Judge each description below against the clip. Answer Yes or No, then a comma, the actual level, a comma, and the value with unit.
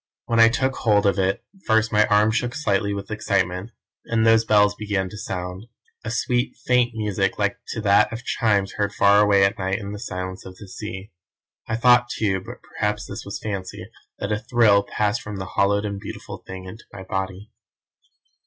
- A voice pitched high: No, low, 105 Hz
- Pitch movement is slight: Yes, narrow, 2.3 semitones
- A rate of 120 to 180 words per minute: No, average, 195 wpm